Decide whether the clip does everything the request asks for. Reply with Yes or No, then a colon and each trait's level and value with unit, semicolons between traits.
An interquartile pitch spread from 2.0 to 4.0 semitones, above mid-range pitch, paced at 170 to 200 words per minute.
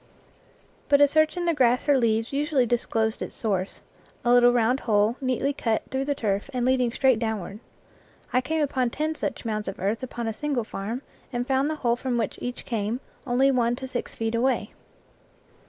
Yes: average, 3.1 semitones; high, 245 Hz; average, 195 wpm